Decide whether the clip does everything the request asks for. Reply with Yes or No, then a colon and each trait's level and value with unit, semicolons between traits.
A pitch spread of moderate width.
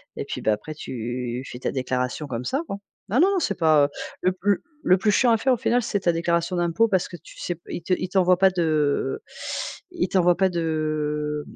Yes: average, 4.5 semitones